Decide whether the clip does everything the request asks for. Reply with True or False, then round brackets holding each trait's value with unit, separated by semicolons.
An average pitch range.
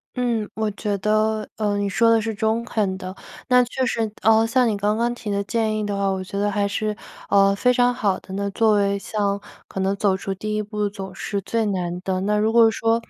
False (2.1 semitones)